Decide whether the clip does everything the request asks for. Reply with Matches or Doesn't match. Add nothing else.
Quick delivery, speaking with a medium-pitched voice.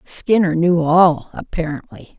Doesn't match